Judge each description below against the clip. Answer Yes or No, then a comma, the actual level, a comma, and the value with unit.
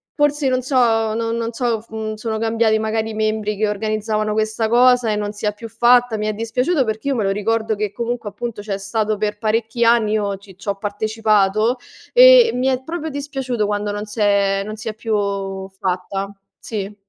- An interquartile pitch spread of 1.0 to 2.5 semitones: Yes, narrow, 2.1 semitones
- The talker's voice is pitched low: No, high, 220 Hz